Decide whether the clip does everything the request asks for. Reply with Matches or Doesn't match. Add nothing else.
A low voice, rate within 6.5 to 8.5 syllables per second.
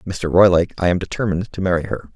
Matches